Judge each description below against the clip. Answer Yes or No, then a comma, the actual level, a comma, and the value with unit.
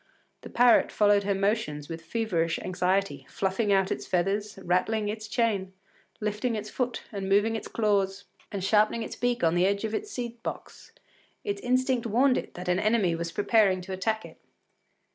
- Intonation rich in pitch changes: No, average, 3.2 semitones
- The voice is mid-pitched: No, high, 205 Hz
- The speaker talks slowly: No, average, 180 wpm